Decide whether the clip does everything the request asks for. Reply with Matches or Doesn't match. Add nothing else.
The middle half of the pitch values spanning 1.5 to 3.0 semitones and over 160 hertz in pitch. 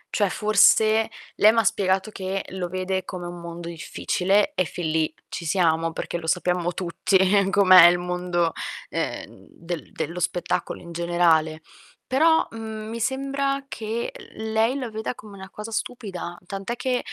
Doesn't match